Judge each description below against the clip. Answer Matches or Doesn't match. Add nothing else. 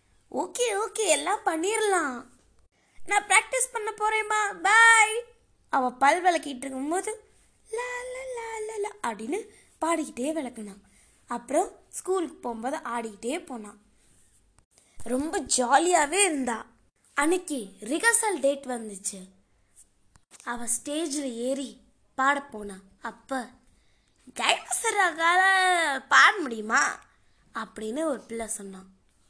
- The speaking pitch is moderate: Doesn't match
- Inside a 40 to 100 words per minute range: Matches